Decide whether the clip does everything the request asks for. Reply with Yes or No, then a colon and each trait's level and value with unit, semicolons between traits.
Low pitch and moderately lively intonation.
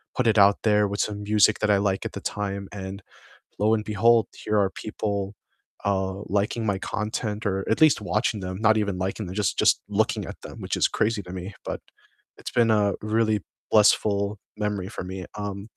No: low, 105 Hz; narrow, 1.5 semitones